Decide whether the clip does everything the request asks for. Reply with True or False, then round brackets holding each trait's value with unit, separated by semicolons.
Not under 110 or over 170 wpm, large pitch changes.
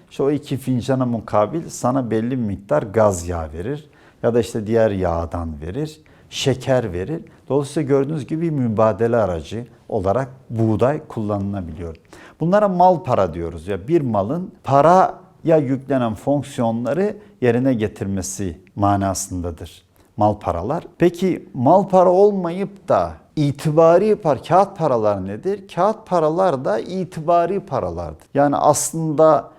True (125 wpm; 7.6 semitones)